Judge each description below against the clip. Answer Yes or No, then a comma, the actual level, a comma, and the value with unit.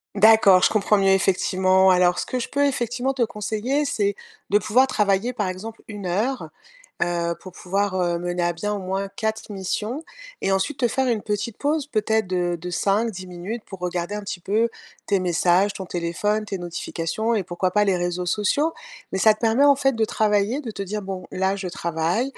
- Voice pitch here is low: No, high, 200 Hz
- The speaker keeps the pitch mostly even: No, average, 3.5 semitones